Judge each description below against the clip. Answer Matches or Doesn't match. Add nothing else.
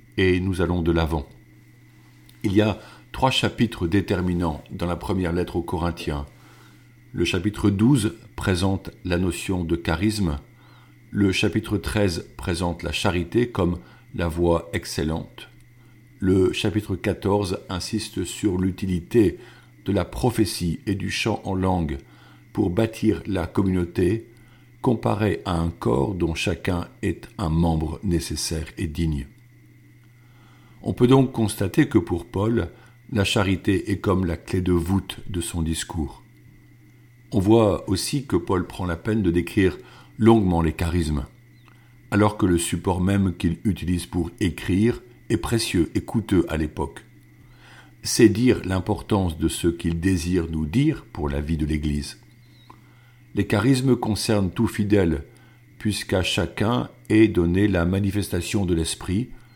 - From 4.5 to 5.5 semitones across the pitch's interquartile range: Matches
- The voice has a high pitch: Doesn't match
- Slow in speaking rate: Matches